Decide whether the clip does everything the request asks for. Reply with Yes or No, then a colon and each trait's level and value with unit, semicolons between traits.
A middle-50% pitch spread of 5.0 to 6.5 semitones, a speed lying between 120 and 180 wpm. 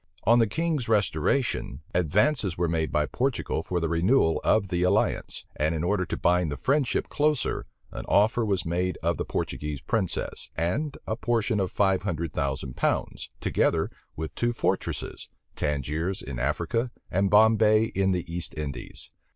Yes: wide, 5.5 semitones; average, 160 wpm